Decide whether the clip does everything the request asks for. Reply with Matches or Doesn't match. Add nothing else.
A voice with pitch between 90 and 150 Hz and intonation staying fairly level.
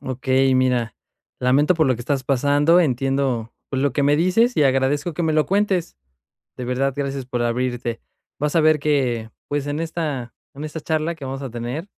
Doesn't match